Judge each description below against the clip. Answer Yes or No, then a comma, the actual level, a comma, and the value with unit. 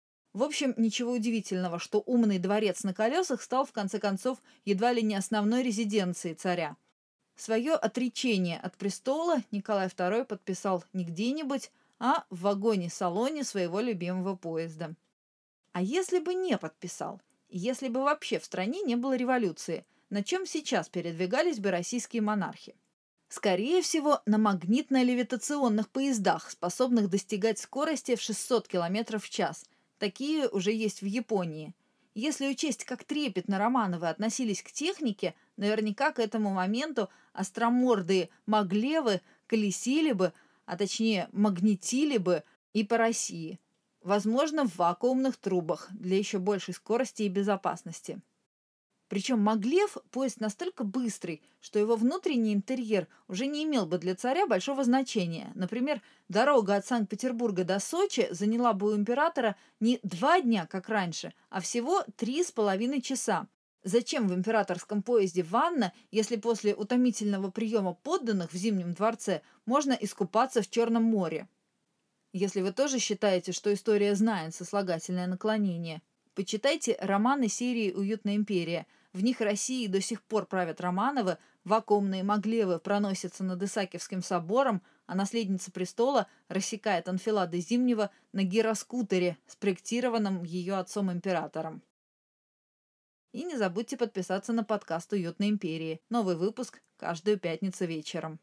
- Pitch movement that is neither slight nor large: Yes, average, 4.4 semitones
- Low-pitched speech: No, high, 215 Hz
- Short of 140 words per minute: Yes, average, 130 wpm